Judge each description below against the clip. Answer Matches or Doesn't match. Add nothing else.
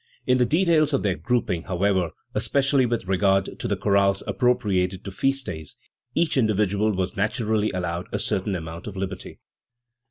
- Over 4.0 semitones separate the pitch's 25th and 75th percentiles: Matches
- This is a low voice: Matches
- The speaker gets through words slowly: Doesn't match